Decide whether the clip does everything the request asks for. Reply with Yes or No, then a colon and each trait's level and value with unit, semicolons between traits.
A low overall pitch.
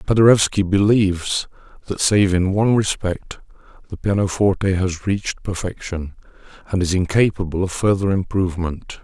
Yes: very low, 95 Hz